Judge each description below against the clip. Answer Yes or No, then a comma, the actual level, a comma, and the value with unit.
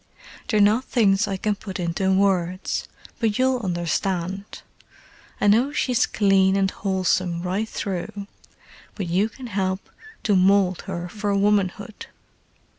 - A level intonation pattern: Yes, narrow, 2.0 semitones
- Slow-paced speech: Yes, slow, 125 wpm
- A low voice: No, high, 195 Hz